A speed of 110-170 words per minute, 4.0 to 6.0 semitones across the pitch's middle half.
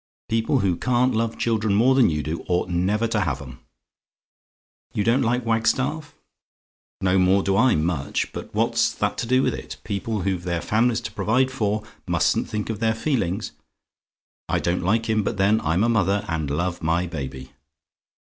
No: average, 180 wpm; average, 4.5 semitones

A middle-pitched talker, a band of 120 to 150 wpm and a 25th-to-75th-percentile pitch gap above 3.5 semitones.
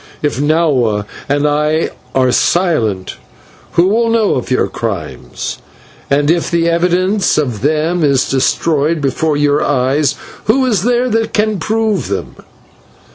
Yes: medium, 155 Hz; slow, 135 wpm; wide, 5.4 semitones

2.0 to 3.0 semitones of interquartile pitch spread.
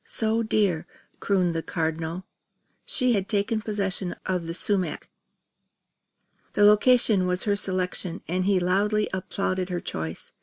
Yes: average, 2.7 semitones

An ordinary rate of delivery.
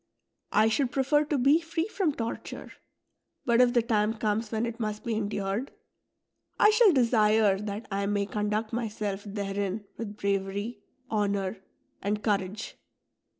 Yes: average, 145 wpm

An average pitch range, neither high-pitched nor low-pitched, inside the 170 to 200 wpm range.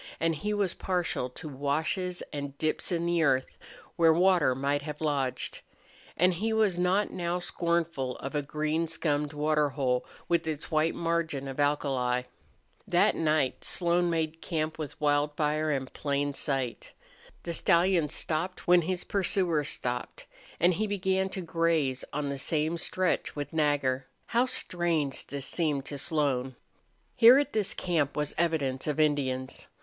No: average, 3.4 semitones; medium, 155 Hz; average, 155 wpm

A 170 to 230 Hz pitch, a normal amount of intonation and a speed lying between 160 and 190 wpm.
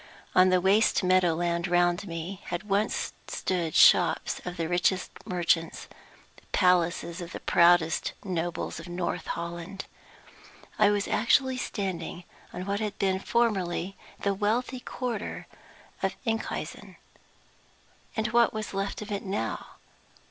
No: medium, 185 Hz; average, 3.0 semitones; slow, 135 wpm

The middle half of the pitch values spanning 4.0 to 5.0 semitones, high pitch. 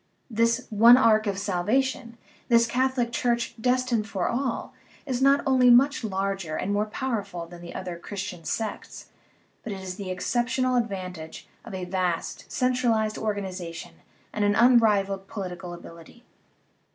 Yes: average, 4.4 semitones; high, 215 Hz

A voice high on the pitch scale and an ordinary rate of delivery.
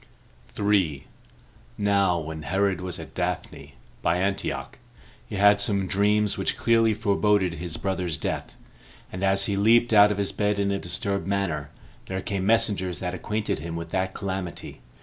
No: low, 100 Hz; average, 160 wpm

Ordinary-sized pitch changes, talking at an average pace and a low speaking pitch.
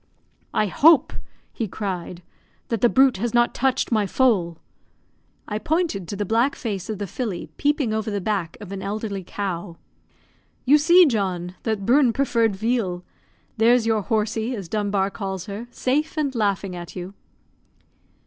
No: average, 4.0 semitones; average, 160 wpm; high, 215 Hz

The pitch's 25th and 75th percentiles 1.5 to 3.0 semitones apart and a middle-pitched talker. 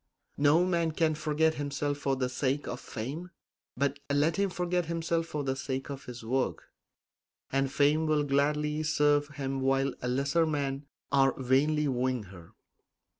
Yes: narrow, 2.5 semitones; medium, 145 Hz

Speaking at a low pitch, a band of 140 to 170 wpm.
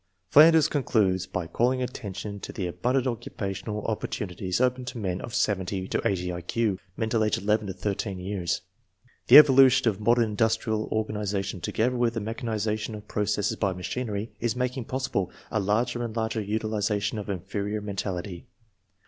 Yes: low, 105 Hz; average, 165 wpm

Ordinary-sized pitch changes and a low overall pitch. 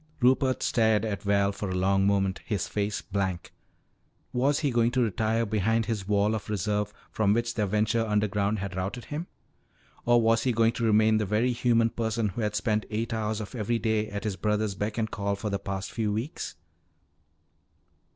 No: narrow, 2.1 semitones; low, 110 Hz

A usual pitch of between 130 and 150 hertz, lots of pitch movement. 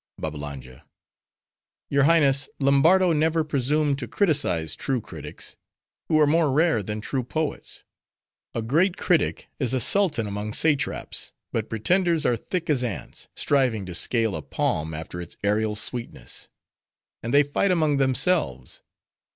Yes: low, 135 Hz; wide, 6.5 semitones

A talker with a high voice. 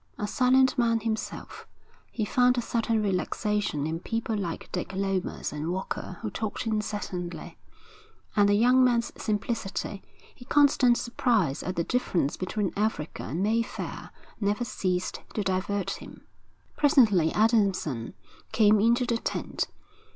Yes: high, 210 Hz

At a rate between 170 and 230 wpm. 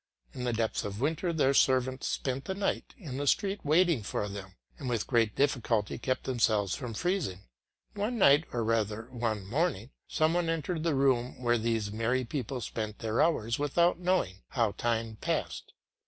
Yes: average, 175 wpm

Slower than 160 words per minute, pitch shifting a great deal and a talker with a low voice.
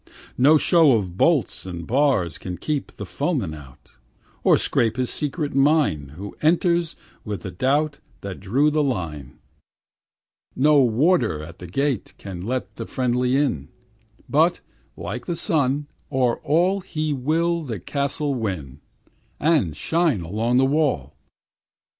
Yes: average, 140 wpm; wide, 8.2 semitones; low, 130 Hz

